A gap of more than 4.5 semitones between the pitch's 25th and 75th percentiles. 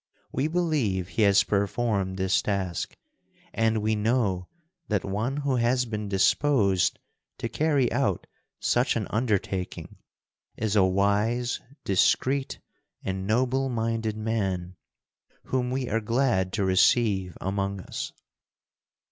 No: average, 4.2 semitones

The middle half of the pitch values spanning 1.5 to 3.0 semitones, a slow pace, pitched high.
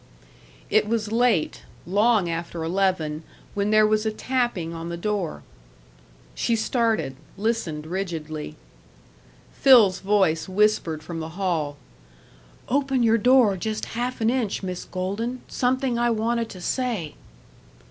No: wide, 5.4 semitones; slow, 125 wpm; high, 210 Hz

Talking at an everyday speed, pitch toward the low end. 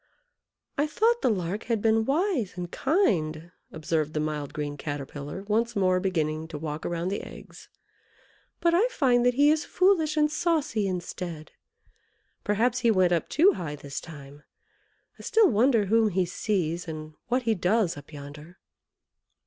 No: average, 160 wpm; high, 190 Hz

